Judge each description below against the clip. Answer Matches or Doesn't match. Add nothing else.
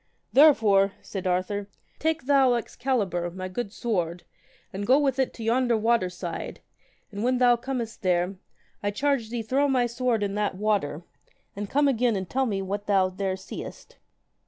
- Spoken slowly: Doesn't match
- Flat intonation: Doesn't match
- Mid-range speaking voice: Doesn't match